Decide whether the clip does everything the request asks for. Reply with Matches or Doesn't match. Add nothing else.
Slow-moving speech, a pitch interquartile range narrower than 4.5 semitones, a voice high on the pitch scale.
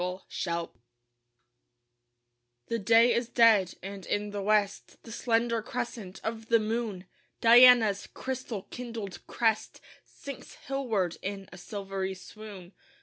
Matches